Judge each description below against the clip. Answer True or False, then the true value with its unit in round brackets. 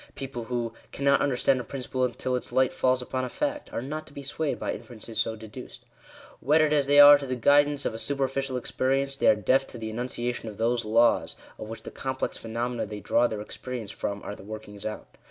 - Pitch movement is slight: False (3.3 semitones)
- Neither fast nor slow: False (225 wpm)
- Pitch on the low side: True (125 Hz)